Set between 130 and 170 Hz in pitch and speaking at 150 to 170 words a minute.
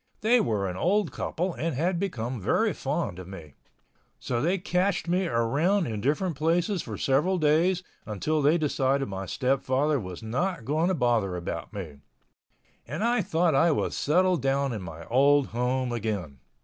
Yes: medium, 140 Hz; average, 165 wpm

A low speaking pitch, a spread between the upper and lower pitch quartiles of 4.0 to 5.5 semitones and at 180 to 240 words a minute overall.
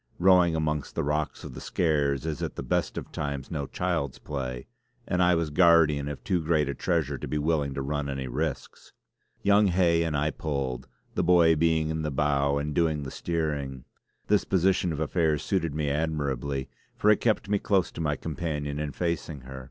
No: very low, 75 Hz; average, 2.9 semitones; average, 200 wpm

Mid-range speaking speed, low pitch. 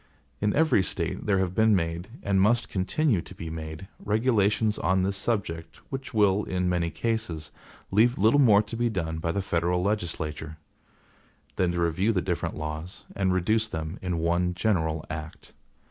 Yes: average, 170 wpm; very low, 95 Hz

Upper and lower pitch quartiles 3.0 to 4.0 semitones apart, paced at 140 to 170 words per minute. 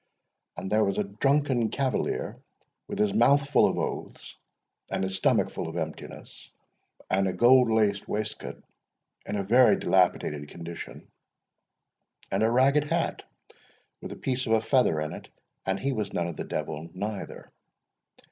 No: average, 5.1 semitones; average, 155 wpm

